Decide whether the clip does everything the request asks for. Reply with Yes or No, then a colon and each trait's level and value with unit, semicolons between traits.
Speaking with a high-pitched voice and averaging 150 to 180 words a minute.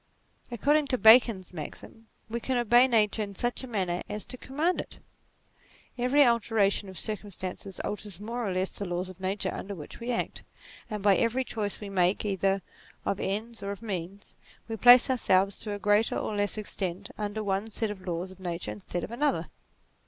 No: high, 205 Hz; average, 190 wpm